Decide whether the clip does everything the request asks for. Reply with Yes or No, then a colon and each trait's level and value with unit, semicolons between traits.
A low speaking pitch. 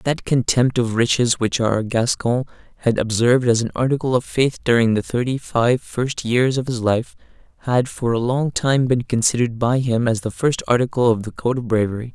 Yes: low, 120 Hz